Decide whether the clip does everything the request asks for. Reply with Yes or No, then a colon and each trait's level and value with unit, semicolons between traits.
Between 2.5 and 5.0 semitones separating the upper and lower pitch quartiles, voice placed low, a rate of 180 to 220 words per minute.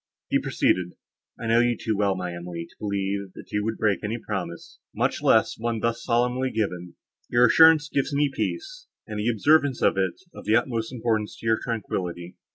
Yes: average, 3.8 semitones; low, 110 Hz; average, 195 wpm